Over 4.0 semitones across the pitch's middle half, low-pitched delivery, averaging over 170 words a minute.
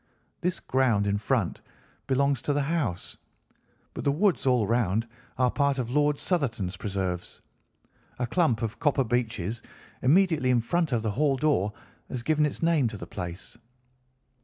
No: average, 5.0 semitones; low, 125 Hz; average, 160 wpm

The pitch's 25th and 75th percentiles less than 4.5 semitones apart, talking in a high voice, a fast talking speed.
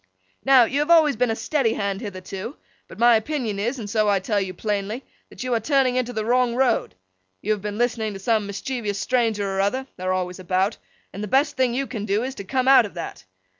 Yes: average, 4.1 semitones; high, 225 Hz; fast, 225 wpm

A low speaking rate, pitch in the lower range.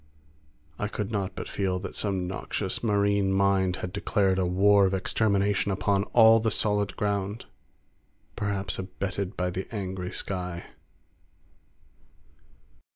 Yes: slow, 125 wpm; low, 100 Hz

